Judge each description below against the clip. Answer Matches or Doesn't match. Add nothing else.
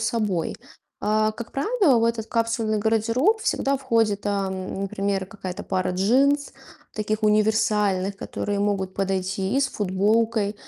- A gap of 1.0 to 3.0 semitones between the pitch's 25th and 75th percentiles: Matches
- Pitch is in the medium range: Doesn't match